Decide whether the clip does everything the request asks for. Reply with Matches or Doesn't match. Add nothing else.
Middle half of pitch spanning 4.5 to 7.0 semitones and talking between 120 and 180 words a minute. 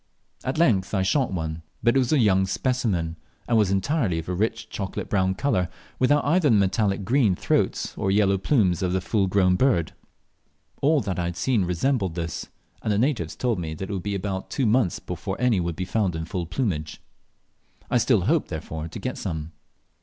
Doesn't match